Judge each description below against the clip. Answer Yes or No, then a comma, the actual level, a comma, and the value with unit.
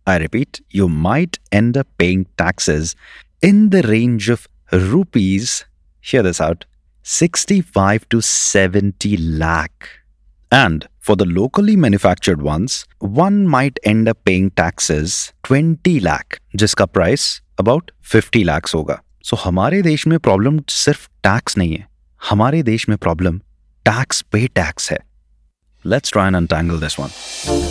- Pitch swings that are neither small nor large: No, wide, 8.0 semitones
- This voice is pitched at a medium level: No, low, 100 Hz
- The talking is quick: No, slow, 135 wpm